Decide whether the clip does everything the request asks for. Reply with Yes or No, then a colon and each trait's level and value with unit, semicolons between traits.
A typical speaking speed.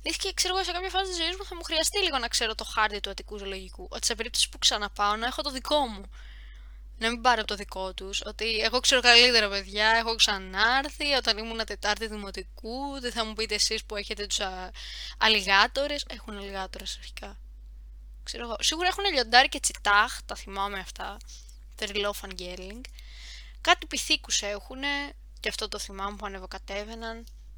No: fast, 180 wpm